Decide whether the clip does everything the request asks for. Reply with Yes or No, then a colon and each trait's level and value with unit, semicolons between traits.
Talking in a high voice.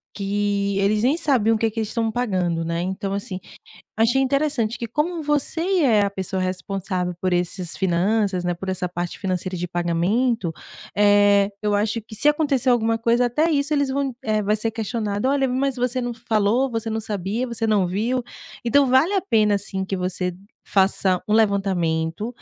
Yes: high, 215 Hz